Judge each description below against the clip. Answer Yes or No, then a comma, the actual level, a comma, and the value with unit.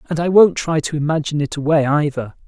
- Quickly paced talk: Yes, fast, 220 wpm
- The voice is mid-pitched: Yes, medium, 150 Hz